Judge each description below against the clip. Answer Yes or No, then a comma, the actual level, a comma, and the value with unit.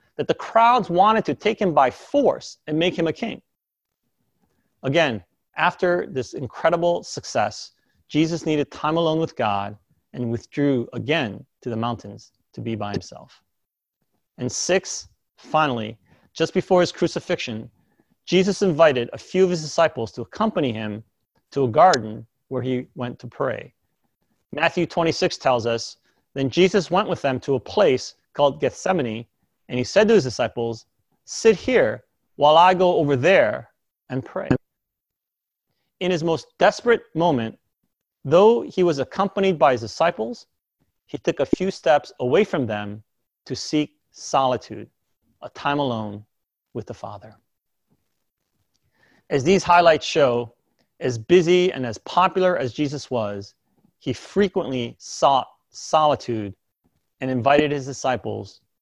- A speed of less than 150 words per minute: Yes, average, 140 wpm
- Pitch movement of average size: No, wide, 7.1 semitones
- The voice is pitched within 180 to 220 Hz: No, medium, 140 Hz